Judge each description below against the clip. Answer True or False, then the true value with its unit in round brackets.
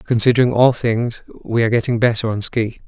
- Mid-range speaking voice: False (115 Hz)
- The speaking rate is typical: True (190 wpm)